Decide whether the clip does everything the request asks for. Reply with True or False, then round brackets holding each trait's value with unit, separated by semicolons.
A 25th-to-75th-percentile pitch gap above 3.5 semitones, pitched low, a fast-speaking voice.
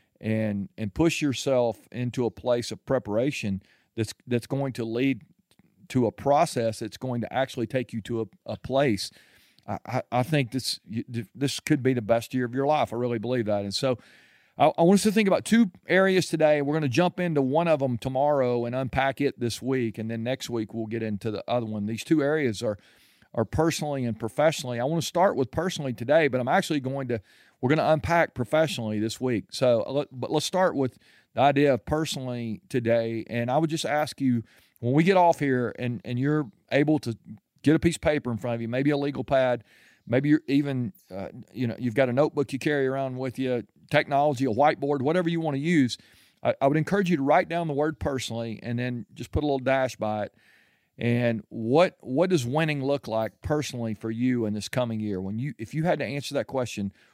True (4.2 semitones; 130 Hz; 225 wpm)